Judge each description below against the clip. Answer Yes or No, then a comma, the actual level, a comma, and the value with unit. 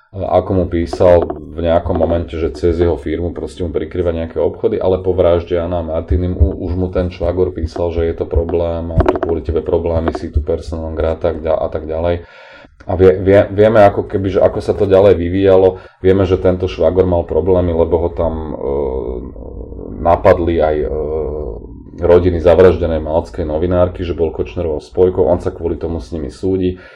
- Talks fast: Yes, fast, 180 wpm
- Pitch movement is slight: Yes, narrow, 1.8 semitones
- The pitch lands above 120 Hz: No, very low, 85 Hz